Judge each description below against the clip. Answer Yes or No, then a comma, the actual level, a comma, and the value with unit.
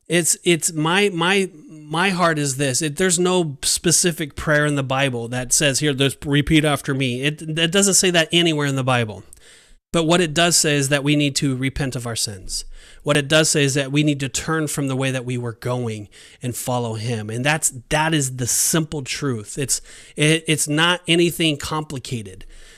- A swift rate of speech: Yes, fast, 210 wpm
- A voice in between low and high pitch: Yes, medium, 150 Hz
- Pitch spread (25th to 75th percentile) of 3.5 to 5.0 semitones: Yes, average, 4.0 semitones